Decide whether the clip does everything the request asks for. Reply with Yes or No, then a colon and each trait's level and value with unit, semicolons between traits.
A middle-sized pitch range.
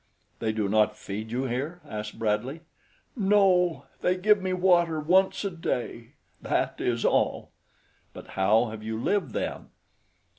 No: wide, 8.8 semitones